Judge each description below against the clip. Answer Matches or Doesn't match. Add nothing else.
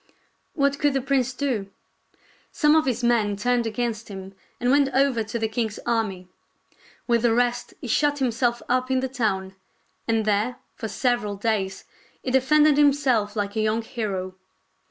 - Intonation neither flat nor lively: Matches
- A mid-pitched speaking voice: Doesn't match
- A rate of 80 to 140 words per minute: Doesn't match